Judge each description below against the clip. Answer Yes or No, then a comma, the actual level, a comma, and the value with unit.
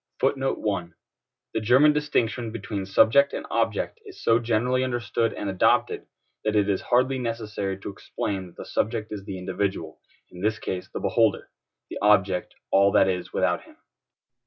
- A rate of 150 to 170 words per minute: Yes, average, 160 wpm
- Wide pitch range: No, average, 3.9 semitones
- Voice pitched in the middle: No, low, 110 Hz